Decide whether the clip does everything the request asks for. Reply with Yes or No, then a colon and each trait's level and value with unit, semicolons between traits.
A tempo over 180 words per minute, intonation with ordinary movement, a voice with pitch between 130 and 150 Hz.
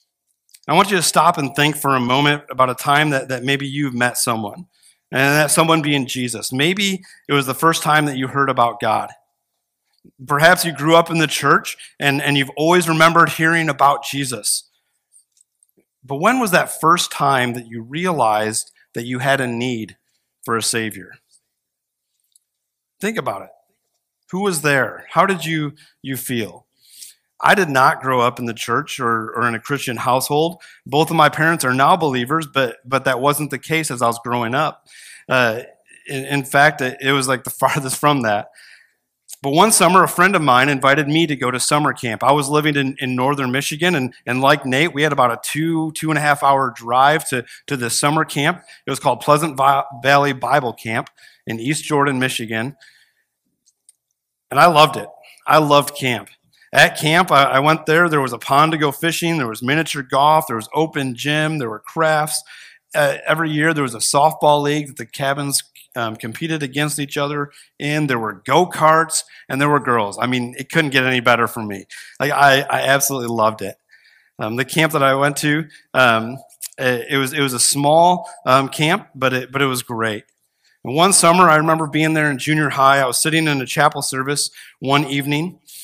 Yes: average, 200 wpm; average, 3.5 semitones; medium, 140 Hz